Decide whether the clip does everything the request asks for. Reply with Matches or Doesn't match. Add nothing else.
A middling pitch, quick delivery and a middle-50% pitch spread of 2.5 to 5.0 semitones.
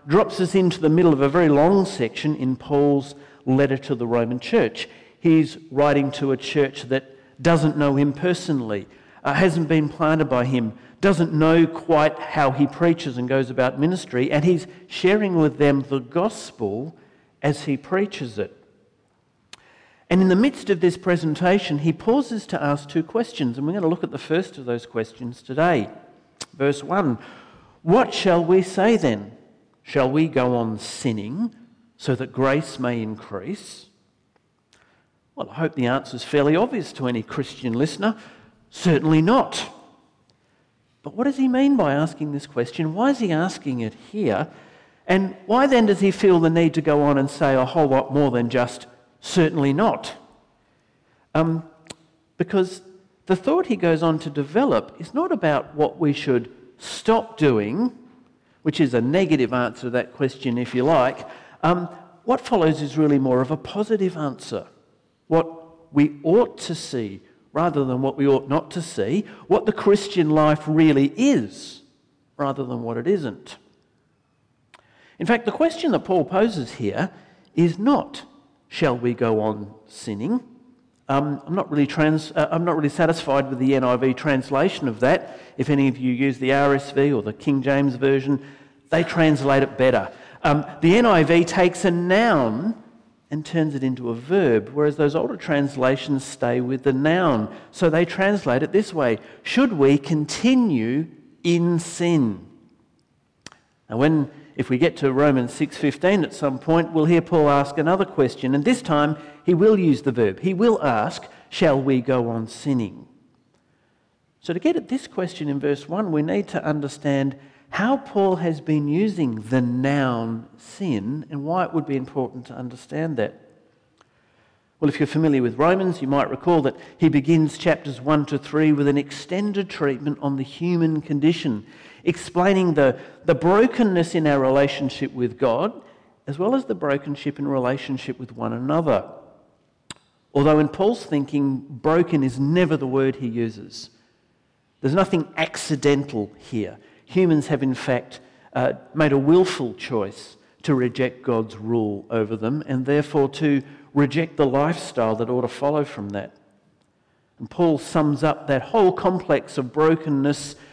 Doesn't match